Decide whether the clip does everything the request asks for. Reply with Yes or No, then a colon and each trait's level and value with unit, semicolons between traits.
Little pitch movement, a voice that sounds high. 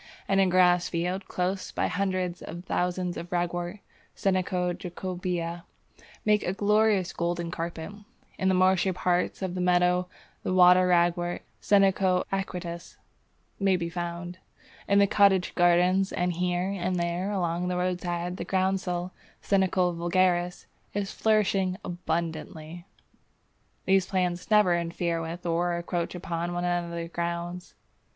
No: narrow, 1.4 semitones; medium, 180 Hz